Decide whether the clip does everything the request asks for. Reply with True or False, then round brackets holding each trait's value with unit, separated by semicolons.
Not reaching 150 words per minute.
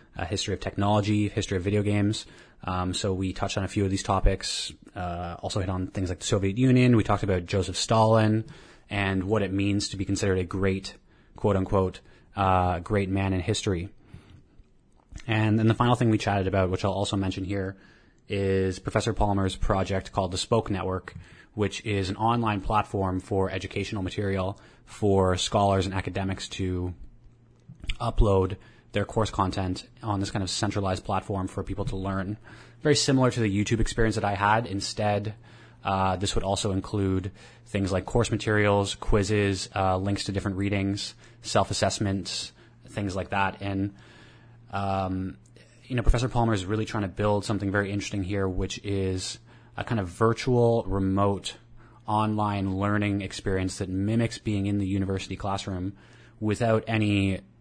False (165 wpm)